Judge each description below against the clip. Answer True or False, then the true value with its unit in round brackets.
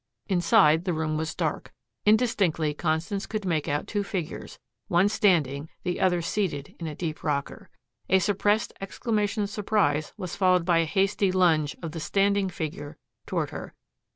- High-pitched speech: False (175 Hz)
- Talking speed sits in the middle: True (160 wpm)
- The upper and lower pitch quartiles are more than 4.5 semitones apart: False (4.2 semitones)